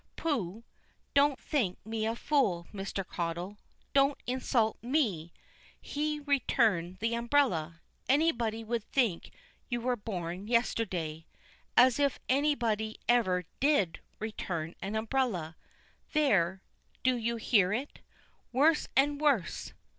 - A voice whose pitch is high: Yes, high, 230 Hz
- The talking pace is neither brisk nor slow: No, slow, 115 wpm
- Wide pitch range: Yes, wide, 6.3 semitones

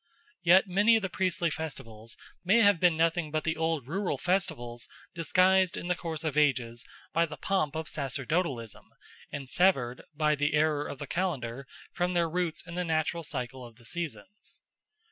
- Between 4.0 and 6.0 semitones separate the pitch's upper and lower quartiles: Yes, average, 4.5 semitones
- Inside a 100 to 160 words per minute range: No, average, 175 wpm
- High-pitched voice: No, medium, 160 Hz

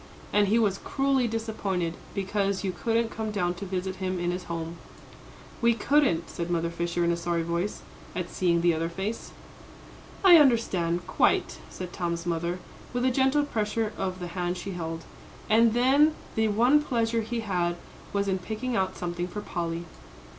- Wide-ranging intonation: No, average, 4.6 semitones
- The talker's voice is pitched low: No, high, 190 Hz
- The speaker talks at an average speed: Yes, average, 175 wpm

